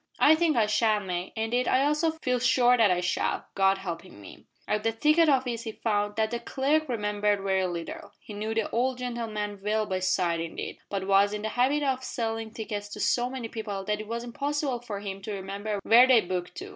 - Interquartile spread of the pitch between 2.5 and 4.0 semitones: Yes, average, 3.7 semitones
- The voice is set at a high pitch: Yes, high, 220 Hz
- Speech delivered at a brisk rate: Yes, fast, 220 wpm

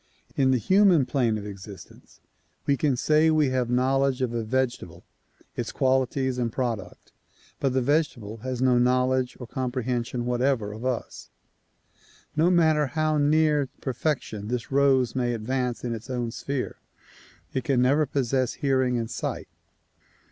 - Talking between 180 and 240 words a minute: No, average, 150 wpm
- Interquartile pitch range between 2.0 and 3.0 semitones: Yes, narrow, 2.4 semitones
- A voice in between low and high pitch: No, low, 130 Hz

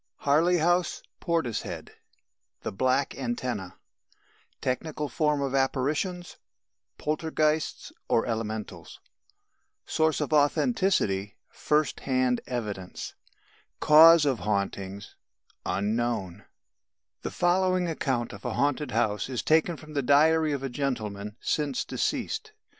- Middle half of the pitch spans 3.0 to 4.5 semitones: No, average, 5.3 semitones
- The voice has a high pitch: No, medium, 140 Hz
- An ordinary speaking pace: No, slow, 105 wpm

